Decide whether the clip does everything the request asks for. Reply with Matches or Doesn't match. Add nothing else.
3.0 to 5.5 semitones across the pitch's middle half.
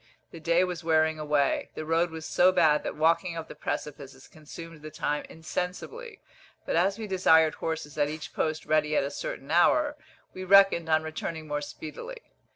Doesn't match